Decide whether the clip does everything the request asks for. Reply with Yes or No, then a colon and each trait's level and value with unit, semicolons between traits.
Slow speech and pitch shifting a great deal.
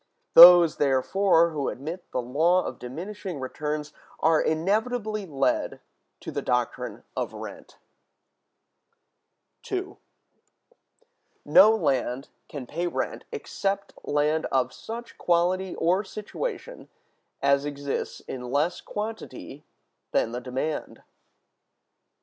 Yes: slow, 105 wpm; wide, 6.1 semitones